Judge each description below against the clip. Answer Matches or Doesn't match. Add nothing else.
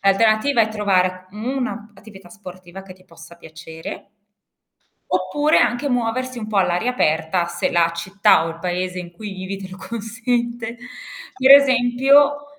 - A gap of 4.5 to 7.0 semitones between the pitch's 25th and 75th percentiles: Matches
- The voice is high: Matches